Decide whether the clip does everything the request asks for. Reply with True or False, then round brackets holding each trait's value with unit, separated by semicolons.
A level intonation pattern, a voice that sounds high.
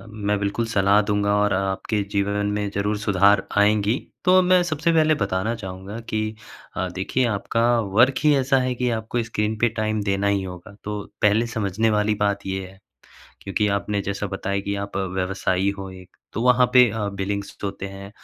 False (2.2 semitones; 105 Hz)